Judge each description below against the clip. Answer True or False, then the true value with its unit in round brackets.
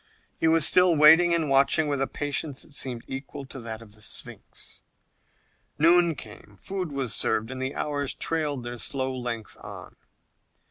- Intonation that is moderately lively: True (4.3 semitones)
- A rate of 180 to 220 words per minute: False (170 wpm)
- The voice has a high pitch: False (140 Hz)